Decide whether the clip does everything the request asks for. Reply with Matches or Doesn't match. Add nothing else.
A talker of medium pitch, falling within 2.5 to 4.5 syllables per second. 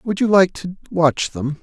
Matches